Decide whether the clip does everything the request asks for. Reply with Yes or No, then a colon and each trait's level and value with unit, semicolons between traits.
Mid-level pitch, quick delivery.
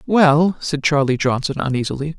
No: medium, 145 Hz; slow, 135 wpm